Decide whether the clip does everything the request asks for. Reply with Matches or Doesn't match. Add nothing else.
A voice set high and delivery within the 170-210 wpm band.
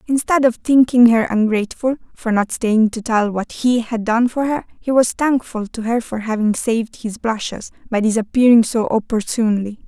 Matches